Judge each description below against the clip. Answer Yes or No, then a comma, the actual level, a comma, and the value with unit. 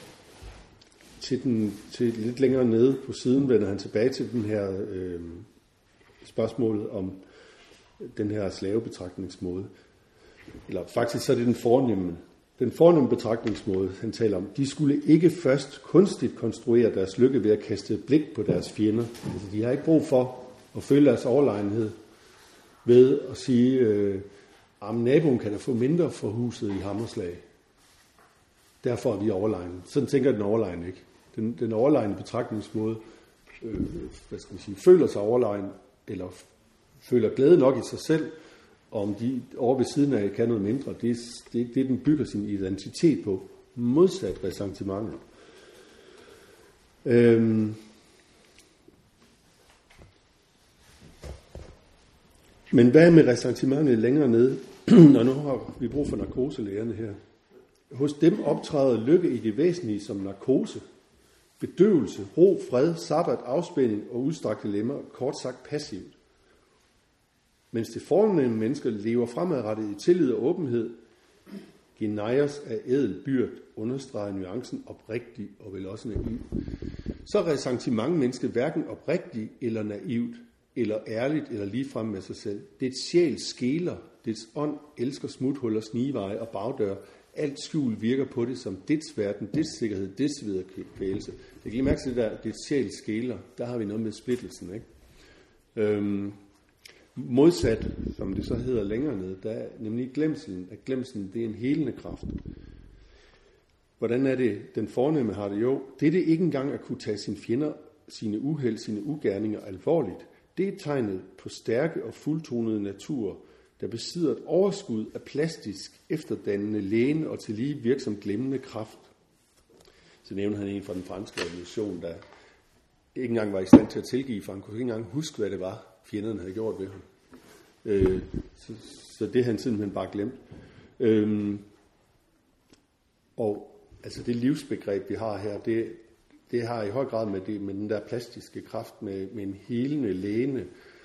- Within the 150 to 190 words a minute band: Yes, average, 155 wpm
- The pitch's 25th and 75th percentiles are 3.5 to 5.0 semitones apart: Yes, average, 4.3 semitones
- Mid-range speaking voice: No, low, 115 Hz